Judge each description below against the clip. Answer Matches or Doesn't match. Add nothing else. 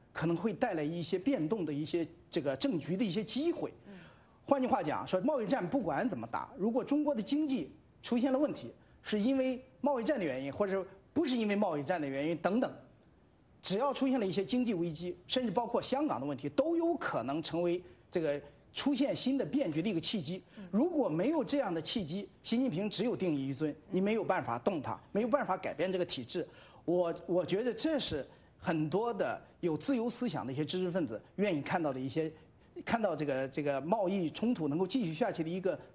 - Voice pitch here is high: Matches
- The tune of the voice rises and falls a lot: Matches